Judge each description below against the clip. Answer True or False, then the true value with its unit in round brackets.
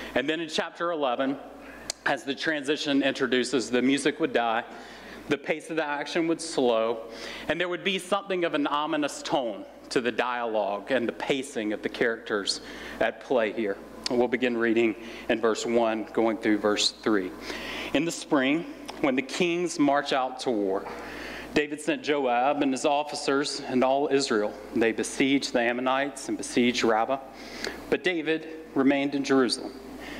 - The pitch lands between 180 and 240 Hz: False (135 Hz)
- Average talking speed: True (165 wpm)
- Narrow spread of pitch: False (4.2 semitones)